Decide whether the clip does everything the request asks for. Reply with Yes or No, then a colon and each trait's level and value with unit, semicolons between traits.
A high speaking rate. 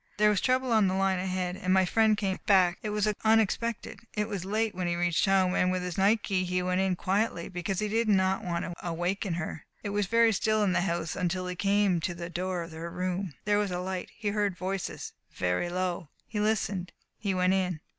Yes: fast, 230 wpm